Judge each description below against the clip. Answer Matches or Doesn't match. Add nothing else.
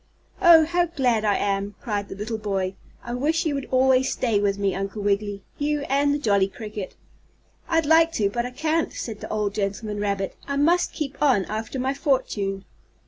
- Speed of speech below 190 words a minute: Doesn't match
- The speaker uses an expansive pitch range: Matches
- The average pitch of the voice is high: Matches